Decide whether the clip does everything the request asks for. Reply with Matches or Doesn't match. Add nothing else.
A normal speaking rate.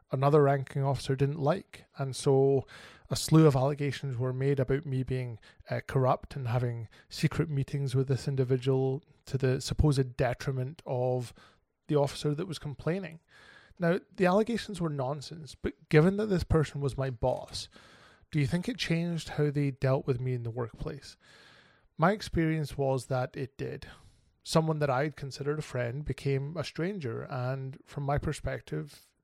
Matches